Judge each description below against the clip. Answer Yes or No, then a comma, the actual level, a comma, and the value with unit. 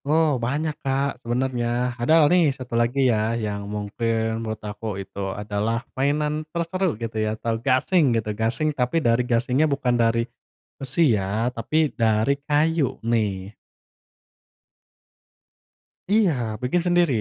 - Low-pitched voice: Yes, low, 120 Hz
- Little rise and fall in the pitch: No, average, 4.8 semitones